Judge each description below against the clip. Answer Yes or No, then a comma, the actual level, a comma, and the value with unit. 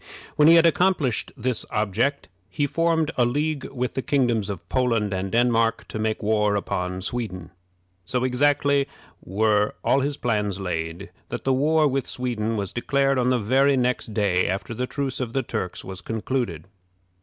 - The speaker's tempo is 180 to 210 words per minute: No, average, 170 wpm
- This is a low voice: Yes, low, 120 Hz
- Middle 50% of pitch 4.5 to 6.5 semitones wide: Yes, average, 4.8 semitones